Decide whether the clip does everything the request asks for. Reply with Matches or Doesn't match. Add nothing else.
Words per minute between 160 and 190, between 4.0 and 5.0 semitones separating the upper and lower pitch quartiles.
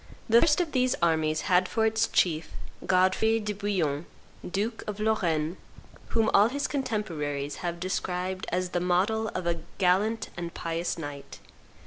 Doesn't match